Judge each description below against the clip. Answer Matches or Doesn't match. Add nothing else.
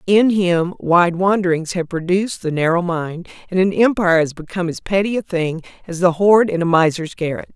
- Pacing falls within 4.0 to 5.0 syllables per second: Doesn't match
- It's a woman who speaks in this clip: Matches